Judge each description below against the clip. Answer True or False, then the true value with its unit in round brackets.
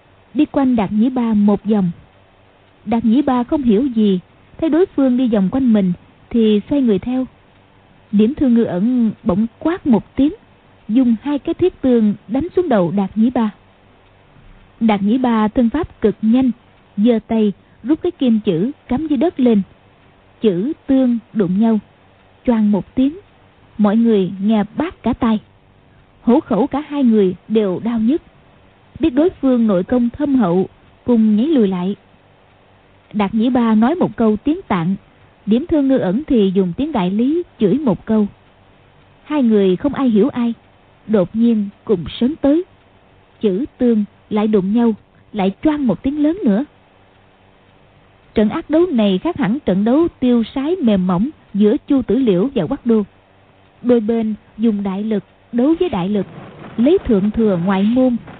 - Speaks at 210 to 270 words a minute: False (170 wpm)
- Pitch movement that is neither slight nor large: True (4.6 semitones)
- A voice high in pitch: True (225 Hz)